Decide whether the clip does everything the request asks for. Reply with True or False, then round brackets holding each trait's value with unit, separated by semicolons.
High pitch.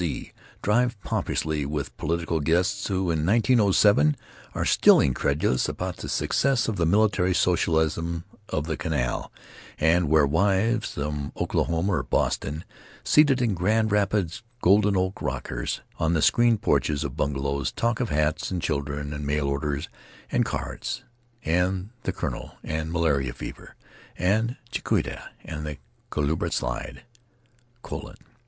False (85 Hz)